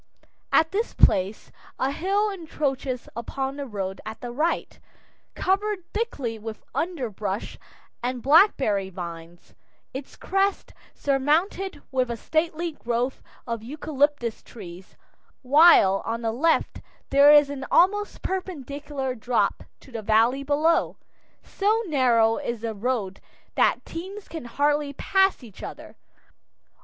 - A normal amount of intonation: No, wide, 6.1 semitones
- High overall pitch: Yes, very high, 275 Hz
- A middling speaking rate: No, slow, 125 wpm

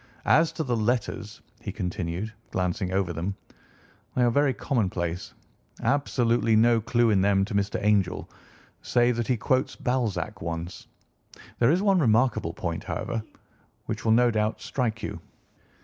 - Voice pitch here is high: No, low, 110 Hz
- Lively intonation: No, average, 4.2 semitones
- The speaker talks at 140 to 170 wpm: Yes, average, 150 wpm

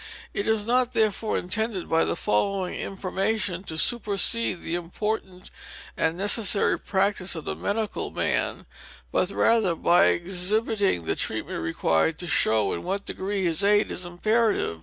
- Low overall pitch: No, high, 195 Hz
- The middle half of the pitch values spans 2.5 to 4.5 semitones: Yes, average, 3.6 semitones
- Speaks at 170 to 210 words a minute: No, average, 145 wpm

